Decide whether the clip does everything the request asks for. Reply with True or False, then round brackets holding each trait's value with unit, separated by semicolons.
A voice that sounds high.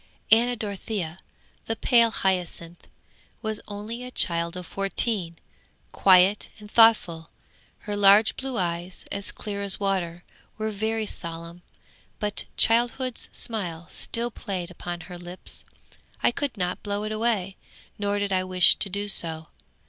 True (200 Hz)